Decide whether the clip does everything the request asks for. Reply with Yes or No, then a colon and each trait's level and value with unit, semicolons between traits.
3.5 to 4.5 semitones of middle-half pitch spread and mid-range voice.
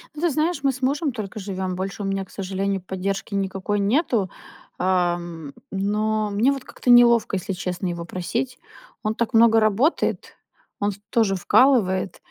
No: average, 4.0 semitones; high, 200 Hz